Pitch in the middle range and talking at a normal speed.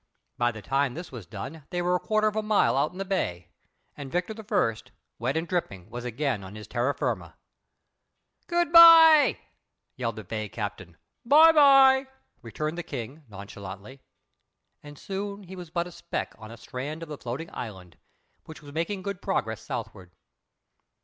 Yes: medium, 150 Hz; average, 170 wpm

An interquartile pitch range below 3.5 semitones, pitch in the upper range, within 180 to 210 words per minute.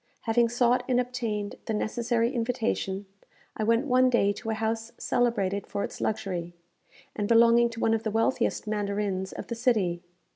No: narrow, 2.6 semitones; high, 225 Hz; average, 170 wpm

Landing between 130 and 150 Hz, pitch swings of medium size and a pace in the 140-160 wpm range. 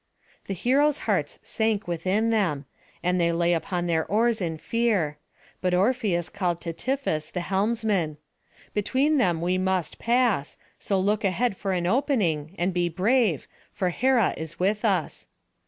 No: high, 190 Hz; average, 4.7 semitones; average, 155 wpm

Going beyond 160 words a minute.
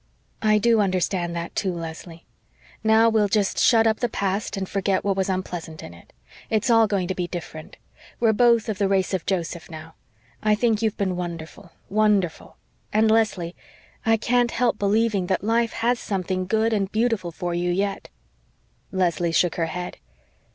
Yes: average, 175 wpm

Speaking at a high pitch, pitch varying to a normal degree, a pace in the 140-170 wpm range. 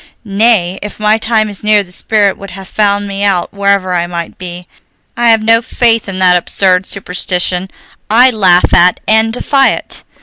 No: high, 200 Hz; average, 3.2 semitones; average, 180 wpm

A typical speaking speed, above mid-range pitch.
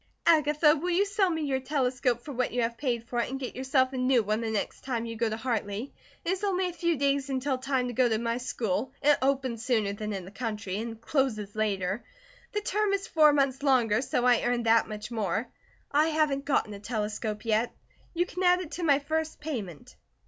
No: fast, 220 wpm; very high, 255 Hz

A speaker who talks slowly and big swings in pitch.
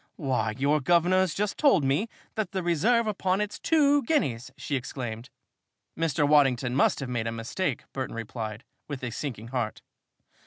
No: average, 160 wpm; wide, 7.4 semitones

